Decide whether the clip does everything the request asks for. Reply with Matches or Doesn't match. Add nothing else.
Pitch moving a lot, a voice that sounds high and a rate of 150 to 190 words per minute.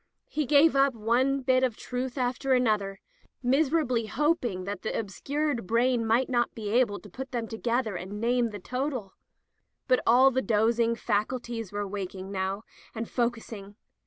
Doesn't match